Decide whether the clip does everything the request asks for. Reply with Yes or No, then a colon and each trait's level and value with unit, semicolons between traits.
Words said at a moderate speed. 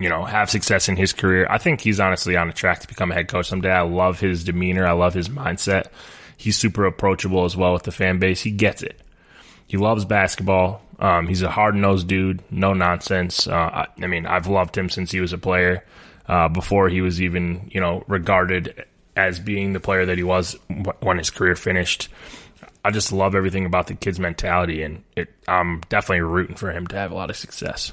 No: fast, 225 wpm